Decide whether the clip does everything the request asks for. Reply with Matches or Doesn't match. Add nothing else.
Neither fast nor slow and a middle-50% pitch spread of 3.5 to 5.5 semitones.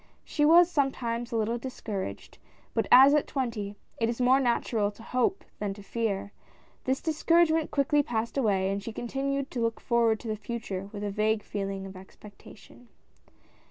Matches